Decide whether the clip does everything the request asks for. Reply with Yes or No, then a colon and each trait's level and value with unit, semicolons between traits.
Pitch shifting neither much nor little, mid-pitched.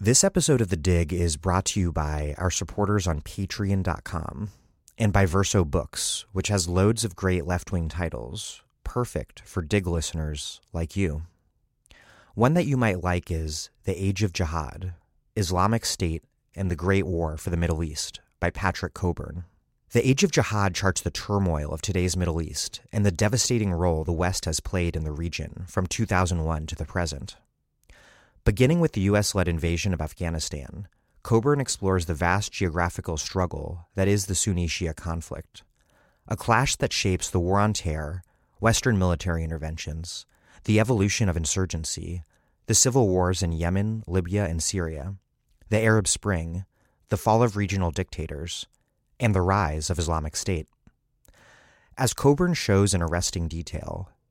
No: average, 3.6 semitones; very low, 90 Hz